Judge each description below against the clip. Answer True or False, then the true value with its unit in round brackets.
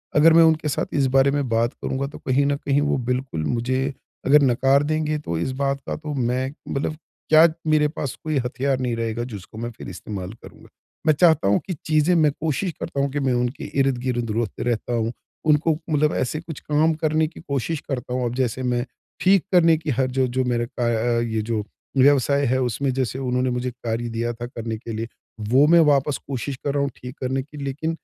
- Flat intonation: False (3.6 semitones)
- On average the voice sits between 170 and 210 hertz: False (135 Hz)